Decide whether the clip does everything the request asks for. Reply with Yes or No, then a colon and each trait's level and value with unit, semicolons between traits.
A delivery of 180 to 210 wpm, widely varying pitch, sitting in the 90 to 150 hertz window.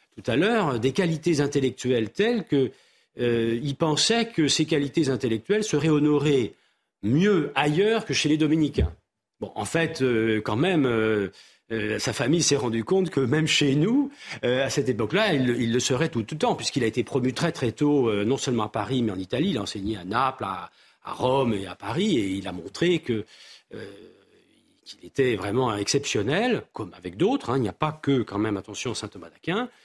Yes: average, 205 wpm; wide, 5.7 semitones; low, 135 Hz